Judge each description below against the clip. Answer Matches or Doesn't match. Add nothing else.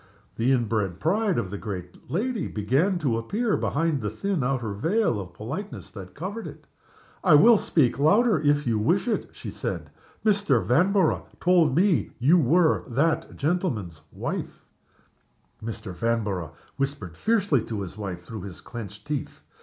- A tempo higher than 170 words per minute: Doesn't match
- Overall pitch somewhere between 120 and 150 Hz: Matches